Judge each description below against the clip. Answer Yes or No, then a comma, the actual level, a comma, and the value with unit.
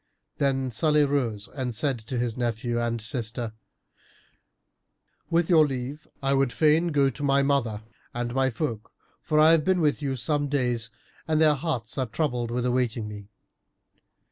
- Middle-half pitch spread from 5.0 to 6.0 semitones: No, average, 3.9 semitones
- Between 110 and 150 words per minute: No, average, 165 wpm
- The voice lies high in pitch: No, low, 130 Hz